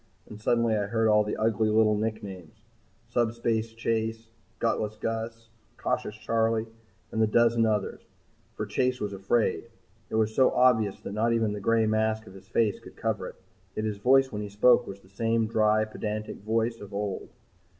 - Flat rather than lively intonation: Yes, narrow, 1.4 semitones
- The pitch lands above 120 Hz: No, low, 110 Hz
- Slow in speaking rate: No, average, 180 wpm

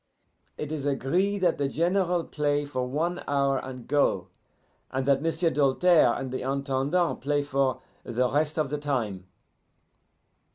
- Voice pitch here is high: No, medium, 145 Hz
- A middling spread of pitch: Yes, average, 3.2 semitones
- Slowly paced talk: No, average, 150 wpm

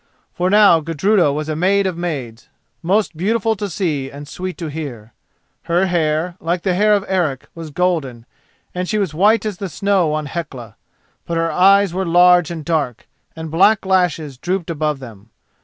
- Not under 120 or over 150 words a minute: No, average, 180 wpm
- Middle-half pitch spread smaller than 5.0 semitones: Yes, average, 3.8 semitones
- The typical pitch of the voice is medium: Yes, medium, 170 Hz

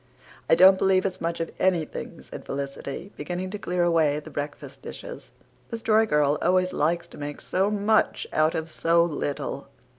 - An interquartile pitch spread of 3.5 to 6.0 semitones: Yes, average, 3.8 semitones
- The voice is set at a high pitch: No, medium, 170 Hz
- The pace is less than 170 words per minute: No, average, 175 wpm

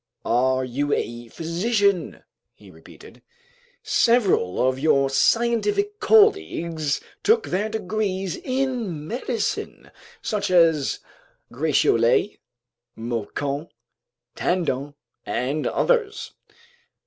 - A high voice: No, medium, 170 Hz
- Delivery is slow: Yes, slow, 80 wpm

